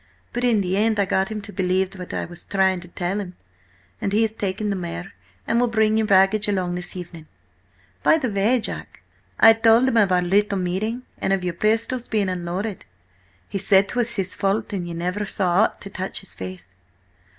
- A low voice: No, high, 195 Hz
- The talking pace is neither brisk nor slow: No, fast, 210 wpm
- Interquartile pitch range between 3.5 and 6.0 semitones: No, average, 3.1 semitones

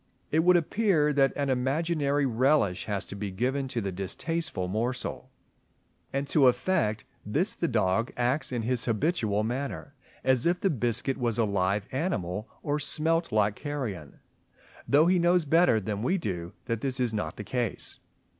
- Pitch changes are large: Yes, wide, 6.0 semitones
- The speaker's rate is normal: Yes, average, 165 wpm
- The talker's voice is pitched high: No, low, 130 Hz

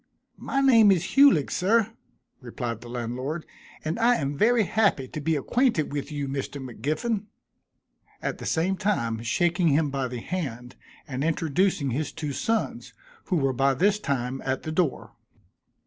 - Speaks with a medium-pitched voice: Yes, medium, 155 Hz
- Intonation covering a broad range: Yes, wide, 6.6 semitones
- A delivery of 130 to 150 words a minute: No, average, 160 wpm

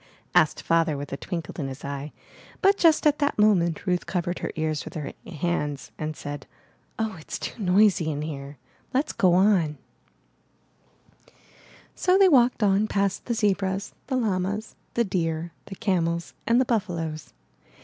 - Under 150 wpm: No, average, 155 wpm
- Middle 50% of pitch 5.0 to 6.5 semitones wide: Yes, average, 5.3 semitones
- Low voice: No, medium, 180 Hz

